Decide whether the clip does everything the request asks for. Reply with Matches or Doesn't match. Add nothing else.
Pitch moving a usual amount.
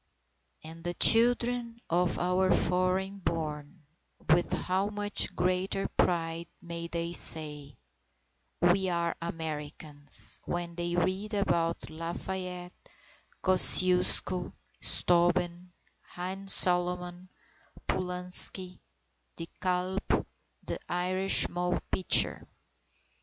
Doesn't match